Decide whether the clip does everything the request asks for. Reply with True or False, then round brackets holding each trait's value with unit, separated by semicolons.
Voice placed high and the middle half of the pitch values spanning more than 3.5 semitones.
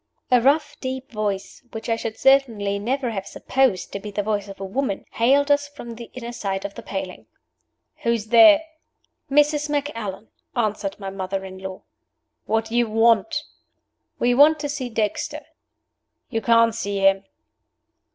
True (225 Hz; 4.9 semitones)